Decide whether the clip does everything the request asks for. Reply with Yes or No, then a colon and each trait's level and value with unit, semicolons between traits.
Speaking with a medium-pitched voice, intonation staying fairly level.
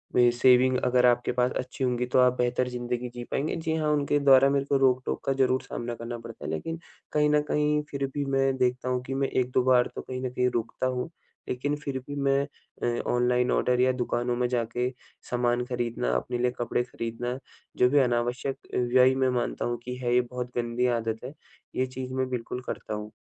No: low, 125 Hz; narrow, 1.4 semitones